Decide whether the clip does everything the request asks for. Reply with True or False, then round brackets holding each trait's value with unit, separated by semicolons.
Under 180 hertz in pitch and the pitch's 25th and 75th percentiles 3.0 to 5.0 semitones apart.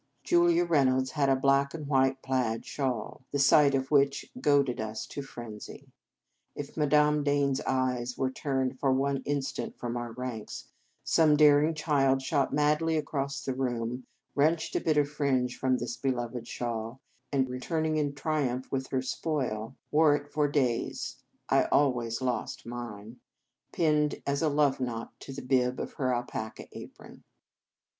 False (135 Hz; 2.6 semitones)